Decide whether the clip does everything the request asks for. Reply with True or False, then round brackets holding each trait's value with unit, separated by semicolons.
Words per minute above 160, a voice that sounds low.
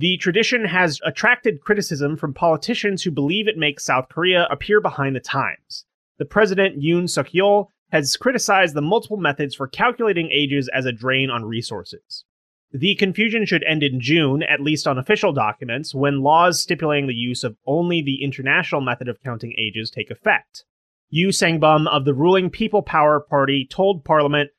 False (170 wpm; 155 Hz)